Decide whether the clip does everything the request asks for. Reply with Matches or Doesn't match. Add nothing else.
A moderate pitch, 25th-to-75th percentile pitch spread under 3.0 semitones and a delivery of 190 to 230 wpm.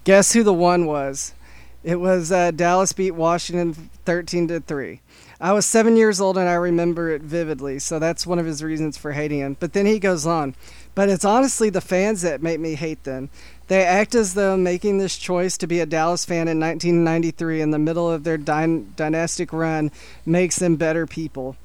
Matches